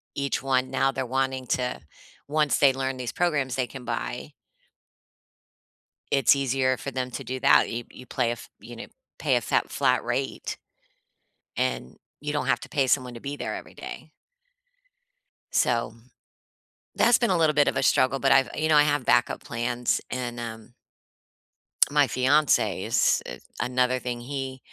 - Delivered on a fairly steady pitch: Yes, narrow, 2.2 semitones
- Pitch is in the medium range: No, low, 130 Hz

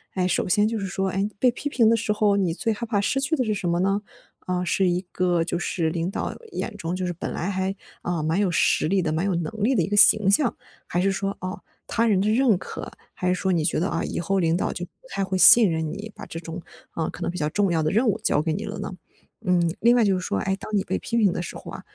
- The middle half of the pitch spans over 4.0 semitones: No, average, 3.2 semitones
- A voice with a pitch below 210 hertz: Yes, high, 190 Hz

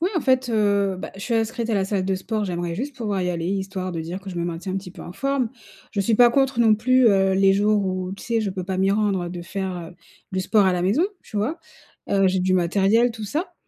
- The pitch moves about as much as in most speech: Yes, average, 3.2 semitones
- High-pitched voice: Yes, high, 195 Hz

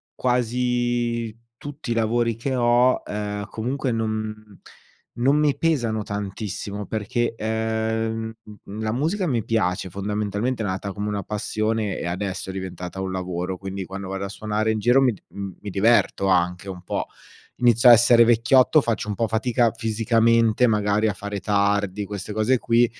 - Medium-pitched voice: No, low, 110 Hz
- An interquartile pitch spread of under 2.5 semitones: No, average, 2.8 semitones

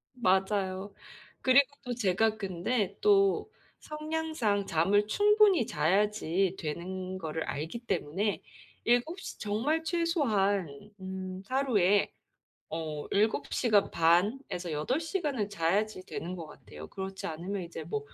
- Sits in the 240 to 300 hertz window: No, high, 200 Hz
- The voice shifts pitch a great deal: Yes, wide, 5.8 semitones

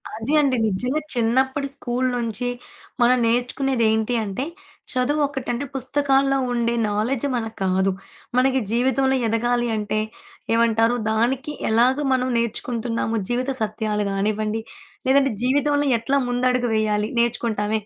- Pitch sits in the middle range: No, high, 240 Hz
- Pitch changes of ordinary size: Yes, average, 3.1 semitones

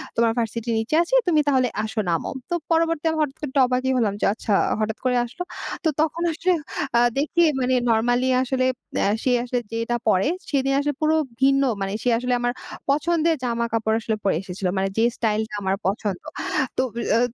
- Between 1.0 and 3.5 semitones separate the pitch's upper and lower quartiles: No, average, 4.3 semitones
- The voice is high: Yes, high, 245 Hz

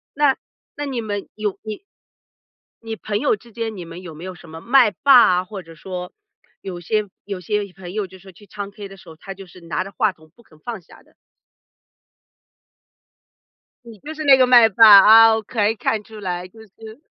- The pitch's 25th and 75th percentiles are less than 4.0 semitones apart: Yes, average, 3.6 semitones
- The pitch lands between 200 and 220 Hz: Yes, high, 205 Hz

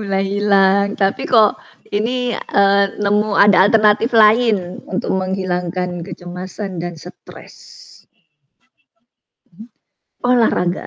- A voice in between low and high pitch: No, high, 200 Hz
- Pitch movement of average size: No, narrow, 2.3 semitones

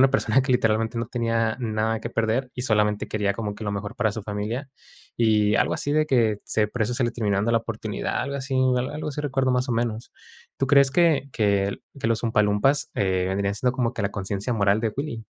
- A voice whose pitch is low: Yes, low, 115 Hz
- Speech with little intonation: No, average, 3.5 semitones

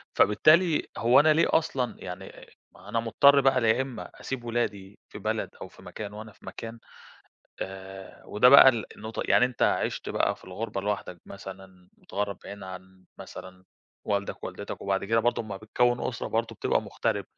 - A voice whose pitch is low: Yes, low, 110 Hz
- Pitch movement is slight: No, average, 4.0 semitones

